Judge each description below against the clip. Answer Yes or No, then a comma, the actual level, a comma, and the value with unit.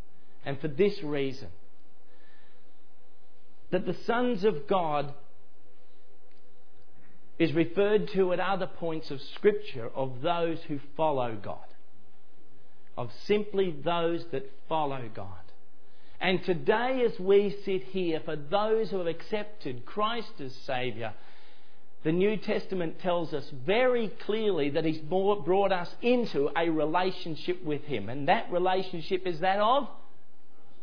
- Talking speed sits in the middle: No, slow, 125 wpm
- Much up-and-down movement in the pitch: Yes, wide, 6.3 semitones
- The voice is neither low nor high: Yes, medium, 165 Hz